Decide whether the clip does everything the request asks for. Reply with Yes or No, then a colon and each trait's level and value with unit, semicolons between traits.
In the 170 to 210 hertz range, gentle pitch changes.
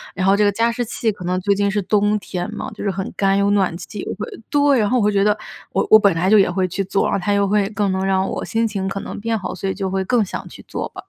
Yes: high, 200 Hz; narrow, 1.6 semitones